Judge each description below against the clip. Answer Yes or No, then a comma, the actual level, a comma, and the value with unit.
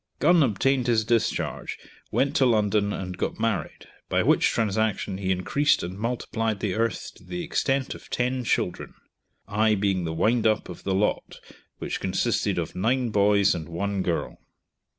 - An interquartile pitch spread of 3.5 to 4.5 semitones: Yes, average, 3.9 semitones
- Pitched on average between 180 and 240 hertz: No, low, 110 Hz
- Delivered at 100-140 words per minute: No, average, 165 wpm